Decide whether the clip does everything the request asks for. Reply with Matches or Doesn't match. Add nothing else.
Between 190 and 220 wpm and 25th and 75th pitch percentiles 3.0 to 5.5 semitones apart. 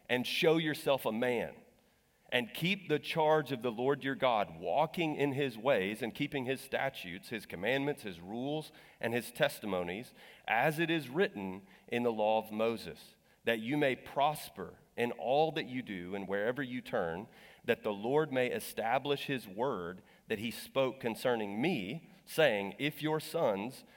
Doesn't match